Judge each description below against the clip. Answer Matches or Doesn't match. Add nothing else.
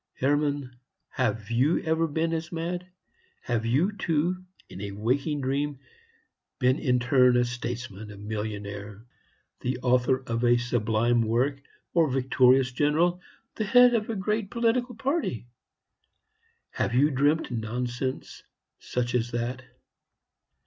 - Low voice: Matches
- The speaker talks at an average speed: Doesn't match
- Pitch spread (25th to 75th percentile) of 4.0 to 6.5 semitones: Matches